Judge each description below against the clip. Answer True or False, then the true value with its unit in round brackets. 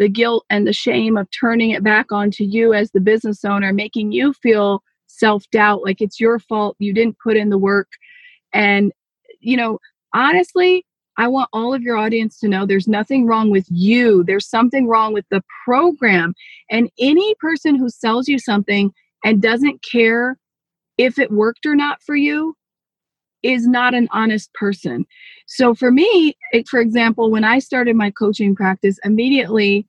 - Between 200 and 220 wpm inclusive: False (175 wpm)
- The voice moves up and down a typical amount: True (3.4 semitones)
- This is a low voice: False (225 Hz)